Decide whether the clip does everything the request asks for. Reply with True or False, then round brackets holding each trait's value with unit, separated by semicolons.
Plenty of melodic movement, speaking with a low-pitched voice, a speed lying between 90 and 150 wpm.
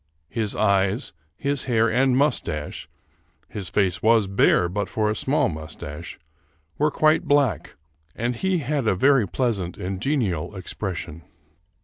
True (6.2 semitones; 110 Hz; 140 wpm)